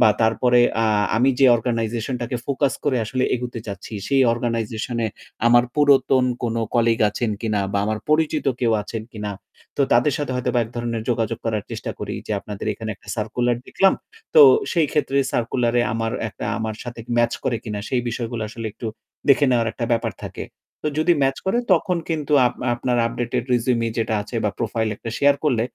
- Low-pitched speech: Yes, low, 120 Hz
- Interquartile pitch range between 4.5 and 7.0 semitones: No, narrow, 2.5 semitones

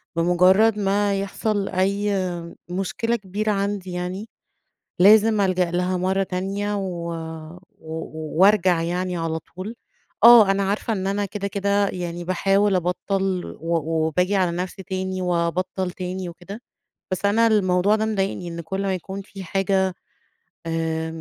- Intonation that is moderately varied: No, narrow, 2.1 semitones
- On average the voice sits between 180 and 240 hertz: Yes, high, 190 Hz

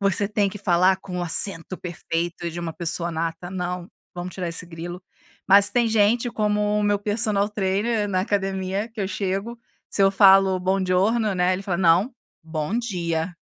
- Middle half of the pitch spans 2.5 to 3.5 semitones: Yes, average, 2.8 semitones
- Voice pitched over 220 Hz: No, high, 190 Hz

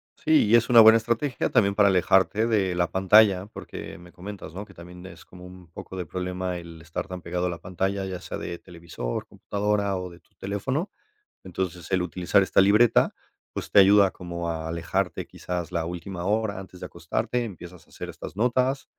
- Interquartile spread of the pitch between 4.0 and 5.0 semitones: No, average, 2.8 semitones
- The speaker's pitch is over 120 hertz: No, very low, 95 Hz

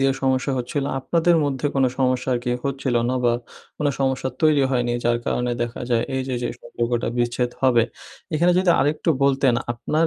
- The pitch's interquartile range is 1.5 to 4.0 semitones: Yes, narrow, 2.5 semitones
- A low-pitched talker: Yes, low, 130 Hz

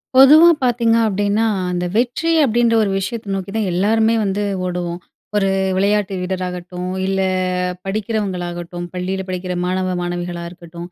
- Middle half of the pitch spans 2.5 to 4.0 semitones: Yes, average, 3.4 semitones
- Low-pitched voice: No, high, 190 Hz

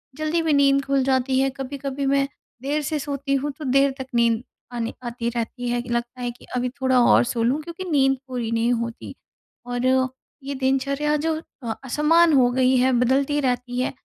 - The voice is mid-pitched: No, very high, 265 Hz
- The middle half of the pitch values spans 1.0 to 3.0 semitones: Yes, narrow, 2.4 semitones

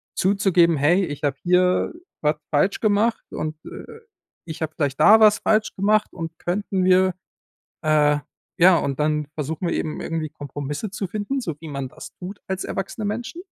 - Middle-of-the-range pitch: Yes, medium, 175 Hz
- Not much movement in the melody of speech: No, average, 4.9 semitones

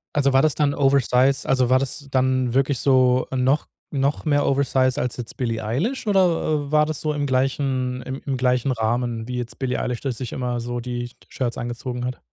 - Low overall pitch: Yes, low, 130 Hz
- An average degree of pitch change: No, narrow, 2.1 semitones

